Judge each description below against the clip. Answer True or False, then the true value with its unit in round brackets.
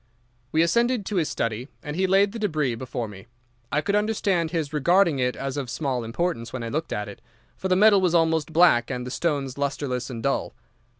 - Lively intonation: True (6.4 semitones)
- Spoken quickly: True (215 wpm)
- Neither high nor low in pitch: True (150 Hz)